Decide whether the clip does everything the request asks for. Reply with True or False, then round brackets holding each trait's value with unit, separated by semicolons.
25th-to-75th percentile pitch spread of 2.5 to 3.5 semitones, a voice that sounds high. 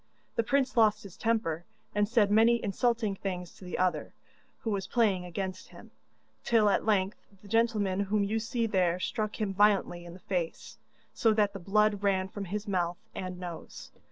True (2.8 semitones; 200 Hz)